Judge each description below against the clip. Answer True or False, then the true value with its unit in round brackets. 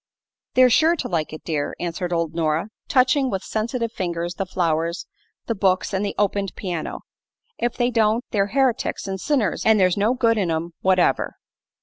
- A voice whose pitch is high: True (195 Hz)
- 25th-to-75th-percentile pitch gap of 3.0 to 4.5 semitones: False (5.2 semitones)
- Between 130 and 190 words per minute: True (180 wpm)